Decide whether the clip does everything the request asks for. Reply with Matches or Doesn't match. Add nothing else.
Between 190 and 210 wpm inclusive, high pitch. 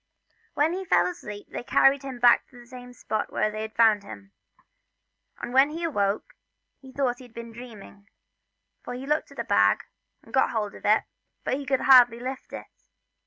Matches